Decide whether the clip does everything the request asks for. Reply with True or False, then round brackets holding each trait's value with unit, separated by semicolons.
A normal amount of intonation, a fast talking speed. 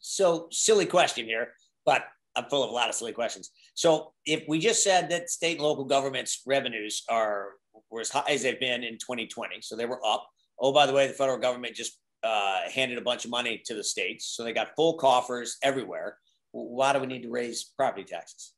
True (4.5 semitones; 220 wpm)